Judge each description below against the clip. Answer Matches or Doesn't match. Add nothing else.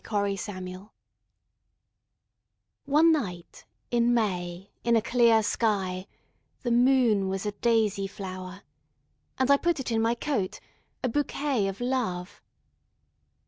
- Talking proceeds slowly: Matches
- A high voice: Matches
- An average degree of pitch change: Matches